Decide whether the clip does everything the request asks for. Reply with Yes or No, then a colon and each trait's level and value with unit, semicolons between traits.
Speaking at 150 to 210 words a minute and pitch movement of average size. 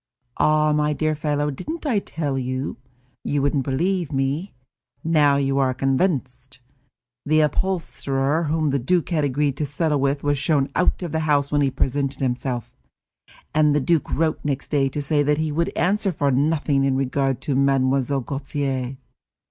No: average, 170 wpm; narrow, 2.3 semitones